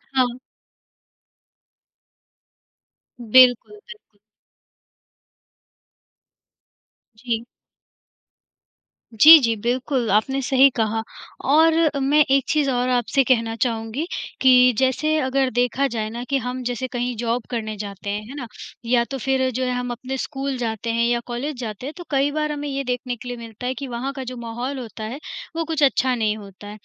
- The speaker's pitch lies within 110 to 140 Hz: No, very high, 250 Hz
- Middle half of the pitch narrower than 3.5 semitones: Yes, average, 2.8 semitones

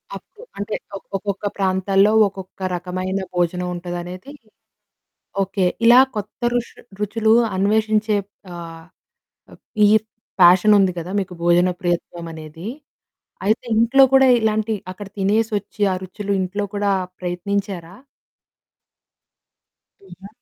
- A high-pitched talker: Yes, high, 195 Hz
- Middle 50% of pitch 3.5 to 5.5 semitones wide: No, average, 2.9 semitones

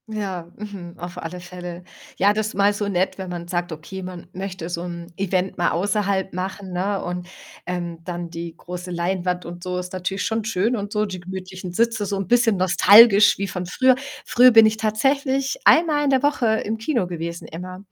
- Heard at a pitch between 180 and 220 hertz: Yes, high, 190 Hz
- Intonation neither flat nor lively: Yes, average, 3.2 semitones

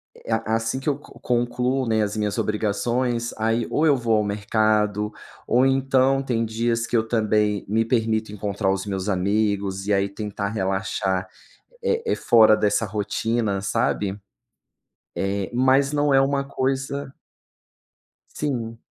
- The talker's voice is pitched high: No, low, 110 Hz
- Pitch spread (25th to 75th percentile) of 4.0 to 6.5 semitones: No, average, 3.5 semitones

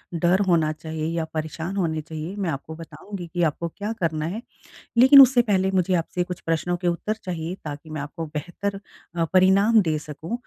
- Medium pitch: Yes, medium, 170 Hz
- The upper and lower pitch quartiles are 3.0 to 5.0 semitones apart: Yes, average, 3.3 semitones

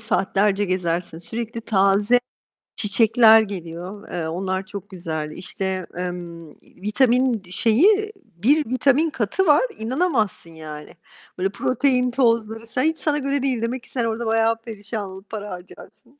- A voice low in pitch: No, high, 220 Hz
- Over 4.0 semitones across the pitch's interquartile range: Yes, average, 4.8 semitones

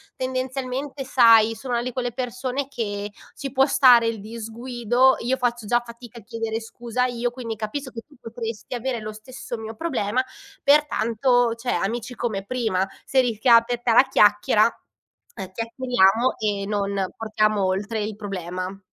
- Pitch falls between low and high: No, high, 235 Hz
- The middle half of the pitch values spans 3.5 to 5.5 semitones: No, average, 2.9 semitones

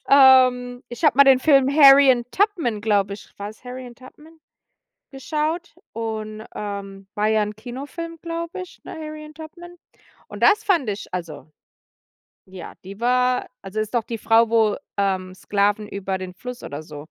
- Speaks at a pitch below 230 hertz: No, high, 240 Hz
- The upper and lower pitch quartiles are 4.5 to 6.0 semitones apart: Yes, wide, 5.6 semitones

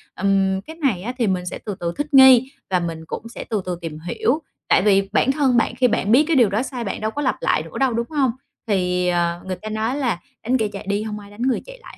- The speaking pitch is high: Yes, high, 215 Hz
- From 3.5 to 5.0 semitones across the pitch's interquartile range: No, wide, 5.6 semitones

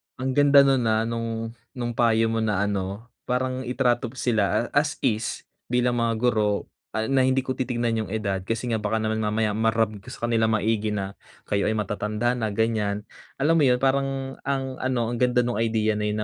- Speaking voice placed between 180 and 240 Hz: No, low, 115 Hz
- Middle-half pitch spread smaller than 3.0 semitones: Yes, narrow, 2.6 semitones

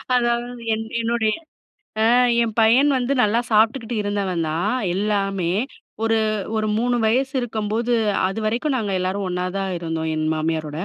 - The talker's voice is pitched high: Yes, high, 215 Hz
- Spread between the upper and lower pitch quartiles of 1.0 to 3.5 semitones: No, average, 4.2 semitones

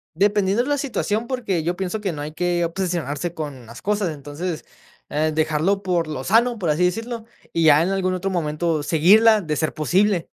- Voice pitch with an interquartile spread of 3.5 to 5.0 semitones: Yes, average, 4.6 semitones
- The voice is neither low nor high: Yes, medium, 175 Hz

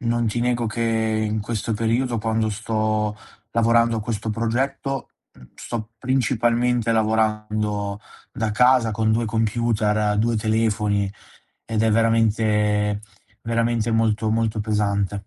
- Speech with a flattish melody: Yes, narrow, 1.6 semitones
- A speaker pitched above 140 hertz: No, low, 110 Hz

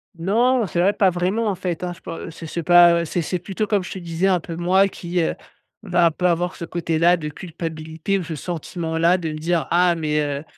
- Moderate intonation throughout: No, narrow, 2.0 semitones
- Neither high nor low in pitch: Yes, medium, 175 Hz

